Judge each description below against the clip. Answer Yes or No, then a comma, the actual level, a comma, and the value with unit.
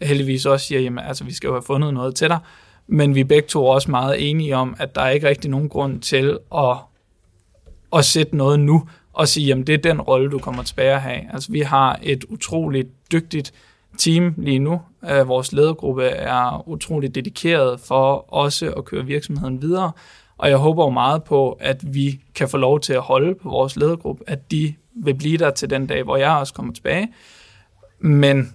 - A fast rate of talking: No, average, 205 wpm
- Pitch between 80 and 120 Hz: No, medium, 140 Hz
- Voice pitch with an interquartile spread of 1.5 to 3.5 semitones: Yes, average, 2.9 semitones